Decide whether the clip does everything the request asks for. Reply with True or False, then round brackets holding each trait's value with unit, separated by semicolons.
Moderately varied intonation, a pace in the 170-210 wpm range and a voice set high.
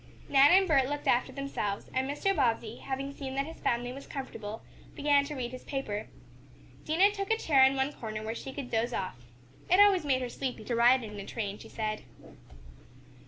True (3.7 semitones; 205 wpm; 265 Hz)